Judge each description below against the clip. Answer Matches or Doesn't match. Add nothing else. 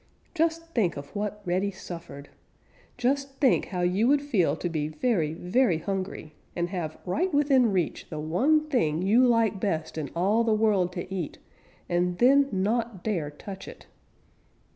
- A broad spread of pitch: Matches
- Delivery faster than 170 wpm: Doesn't match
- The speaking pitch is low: Doesn't match